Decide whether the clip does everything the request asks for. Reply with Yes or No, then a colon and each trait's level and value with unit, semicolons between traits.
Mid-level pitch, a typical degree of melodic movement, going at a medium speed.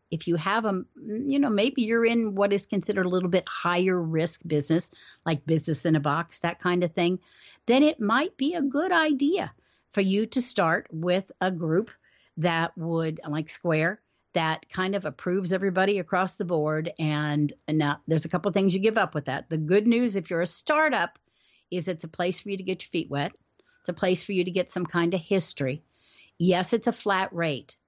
No: medium, 180 Hz; average, 3.6 semitones; fast, 215 wpm